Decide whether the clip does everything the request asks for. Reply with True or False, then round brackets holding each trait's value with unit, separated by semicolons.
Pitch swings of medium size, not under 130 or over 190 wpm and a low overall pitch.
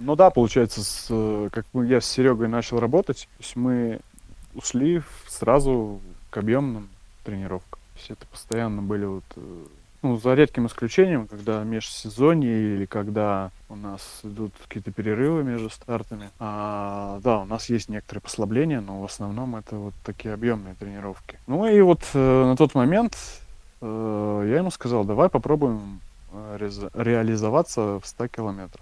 True (3.4 semitones; 145 wpm; 110 Hz)